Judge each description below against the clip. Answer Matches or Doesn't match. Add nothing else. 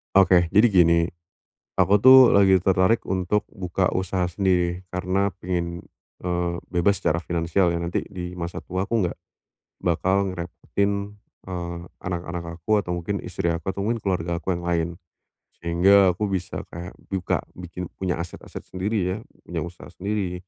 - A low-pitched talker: Matches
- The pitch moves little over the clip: Matches